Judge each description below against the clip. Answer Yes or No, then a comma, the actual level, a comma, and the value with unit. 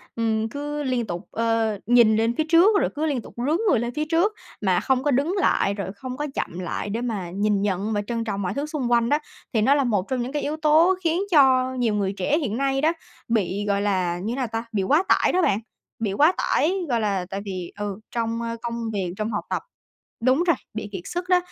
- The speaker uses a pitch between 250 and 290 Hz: No, high, 235 Hz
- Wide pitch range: Yes, wide, 5.8 semitones